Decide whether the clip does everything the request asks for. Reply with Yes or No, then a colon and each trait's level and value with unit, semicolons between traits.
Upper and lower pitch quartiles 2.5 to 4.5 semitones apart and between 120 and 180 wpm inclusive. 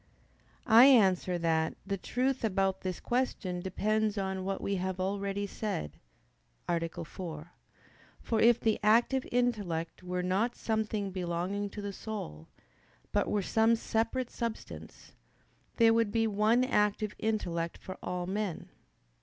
Yes: average, 3.5 semitones; slow, 135 wpm